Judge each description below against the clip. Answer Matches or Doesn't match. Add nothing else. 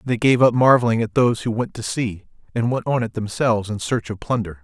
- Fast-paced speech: Matches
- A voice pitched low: Matches